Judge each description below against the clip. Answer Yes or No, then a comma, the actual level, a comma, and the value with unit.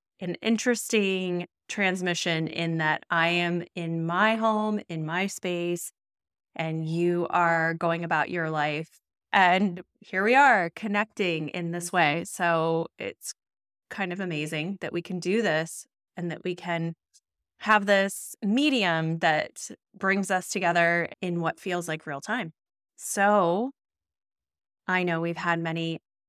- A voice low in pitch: No, medium, 175 Hz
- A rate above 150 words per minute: No, average, 140 wpm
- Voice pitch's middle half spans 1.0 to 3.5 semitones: Yes, average, 3.2 semitones